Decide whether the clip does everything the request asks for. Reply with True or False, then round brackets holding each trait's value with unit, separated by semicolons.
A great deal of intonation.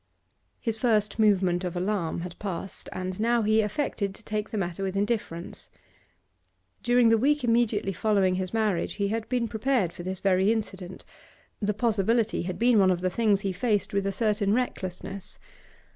False (3.1 semitones)